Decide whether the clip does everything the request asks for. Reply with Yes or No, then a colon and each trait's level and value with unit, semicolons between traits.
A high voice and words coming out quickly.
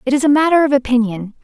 Yes: very high, 265 Hz; fast, 250 wpm